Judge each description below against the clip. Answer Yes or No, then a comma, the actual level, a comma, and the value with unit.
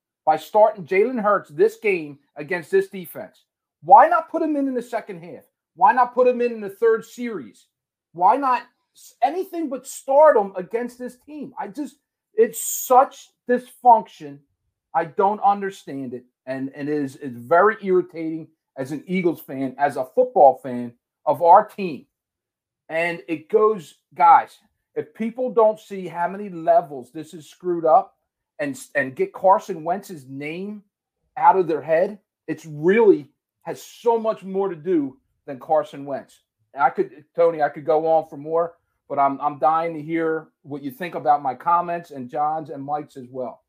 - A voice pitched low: No, medium, 180 Hz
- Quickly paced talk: No, average, 175 wpm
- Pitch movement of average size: No, wide, 8.1 semitones